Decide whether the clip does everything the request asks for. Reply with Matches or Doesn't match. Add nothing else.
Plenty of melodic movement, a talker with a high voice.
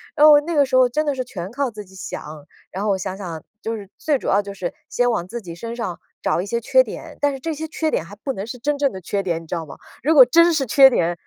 Matches